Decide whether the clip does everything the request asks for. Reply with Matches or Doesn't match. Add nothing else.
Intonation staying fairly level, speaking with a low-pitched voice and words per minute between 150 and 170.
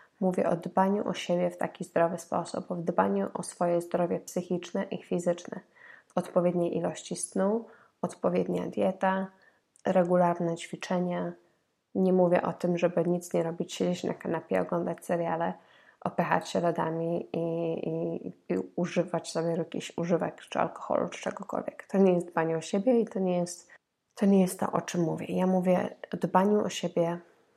Doesn't match